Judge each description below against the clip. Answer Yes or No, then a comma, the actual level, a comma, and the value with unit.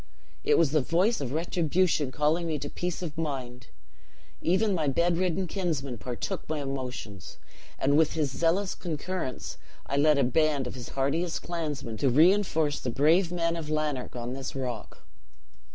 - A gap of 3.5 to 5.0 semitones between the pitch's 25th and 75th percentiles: Yes, average, 4.0 semitones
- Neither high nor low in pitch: Yes, medium, 155 Hz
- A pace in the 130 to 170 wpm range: Yes, average, 160 wpm